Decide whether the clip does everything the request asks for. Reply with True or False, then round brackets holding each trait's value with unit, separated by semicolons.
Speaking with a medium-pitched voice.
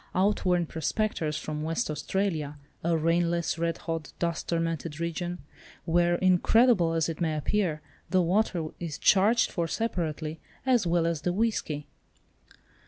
True (170 Hz)